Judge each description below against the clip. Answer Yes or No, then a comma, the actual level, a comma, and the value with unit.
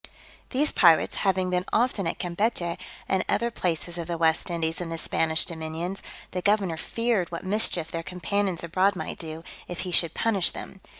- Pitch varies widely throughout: No, average, 2.9 semitones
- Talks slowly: No, average, 180 wpm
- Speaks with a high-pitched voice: No, medium, 175 Hz